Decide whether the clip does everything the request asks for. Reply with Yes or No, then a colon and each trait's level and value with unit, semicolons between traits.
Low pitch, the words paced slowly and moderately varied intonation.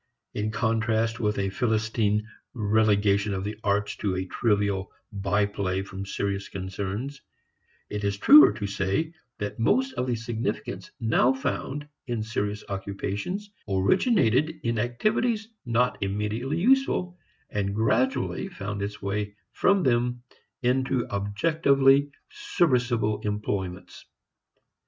Yes: low, 110 Hz; slow, 120 wpm; average, 4.2 semitones